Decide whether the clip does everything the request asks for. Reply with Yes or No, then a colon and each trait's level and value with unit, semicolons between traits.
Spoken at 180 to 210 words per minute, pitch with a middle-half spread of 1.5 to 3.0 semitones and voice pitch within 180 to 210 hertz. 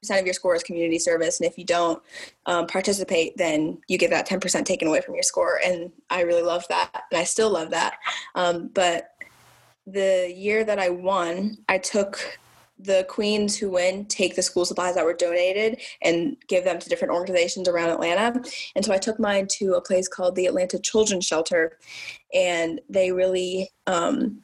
Yes: average, 190 wpm; narrow, 2.6 semitones; medium, 185 Hz